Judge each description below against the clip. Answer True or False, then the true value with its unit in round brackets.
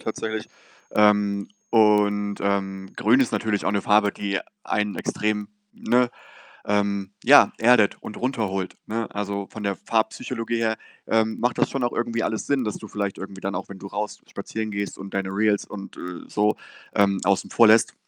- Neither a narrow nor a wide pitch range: False (1.9 semitones)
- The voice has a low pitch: True (105 Hz)